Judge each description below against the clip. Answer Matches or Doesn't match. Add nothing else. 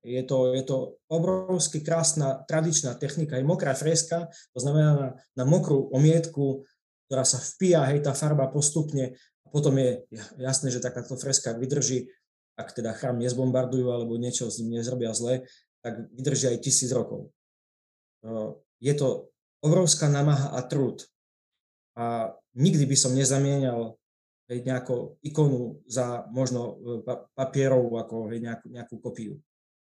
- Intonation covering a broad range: Doesn't match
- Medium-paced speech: Matches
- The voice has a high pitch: Doesn't match